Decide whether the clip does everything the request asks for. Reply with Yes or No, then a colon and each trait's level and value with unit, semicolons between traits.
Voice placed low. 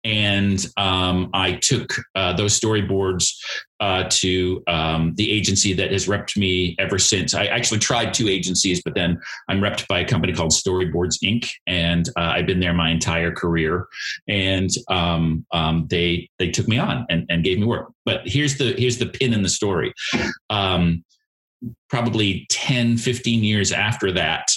Yes: very low, 95 Hz